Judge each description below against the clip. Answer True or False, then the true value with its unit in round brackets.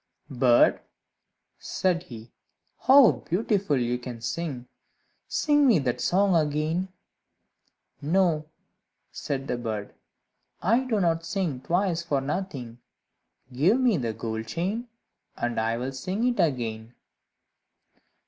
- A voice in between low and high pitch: True (155 Hz)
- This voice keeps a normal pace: False (115 wpm)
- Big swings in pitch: True (7.5 semitones)